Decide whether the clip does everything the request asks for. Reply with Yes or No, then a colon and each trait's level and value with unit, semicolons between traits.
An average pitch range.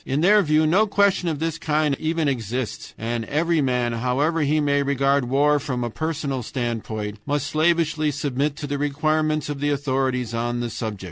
Yes: average, 3.6 semitones